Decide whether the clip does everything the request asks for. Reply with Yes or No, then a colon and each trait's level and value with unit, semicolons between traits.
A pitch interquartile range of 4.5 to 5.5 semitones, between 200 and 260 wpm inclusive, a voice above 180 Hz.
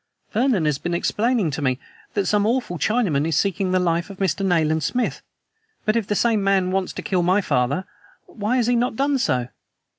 Yes: average, 5.1 semitones; fast, 205 wpm; high, 190 Hz